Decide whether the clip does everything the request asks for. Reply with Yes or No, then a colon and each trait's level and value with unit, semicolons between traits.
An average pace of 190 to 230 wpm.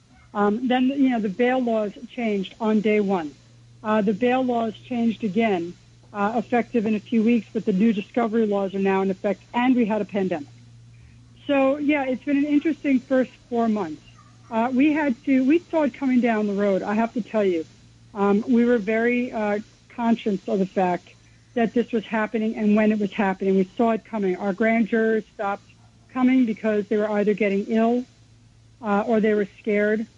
Yes: average, 200 wpm